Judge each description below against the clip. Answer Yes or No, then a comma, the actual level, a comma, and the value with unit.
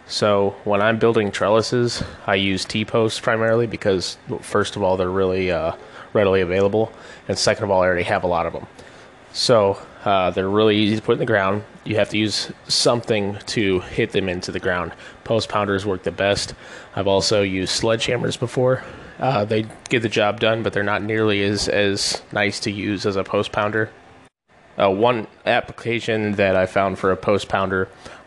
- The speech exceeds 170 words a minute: Yes, average, 190 wpm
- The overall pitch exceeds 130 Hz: No, low, 100 Hz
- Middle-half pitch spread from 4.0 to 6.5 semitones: No, narrow, 2.6 semitones